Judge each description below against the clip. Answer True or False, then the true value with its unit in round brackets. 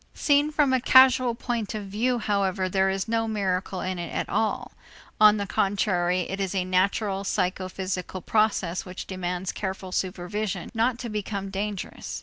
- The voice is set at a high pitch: True (195 Hz)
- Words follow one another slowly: False (160 wpm)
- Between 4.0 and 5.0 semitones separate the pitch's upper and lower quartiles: False (2.8 semitones)